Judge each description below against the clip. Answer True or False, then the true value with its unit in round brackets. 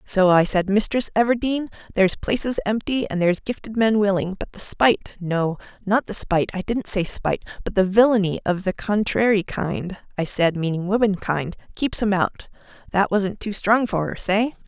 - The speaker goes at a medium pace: True (170 wpm)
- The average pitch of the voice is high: True (200 Hz)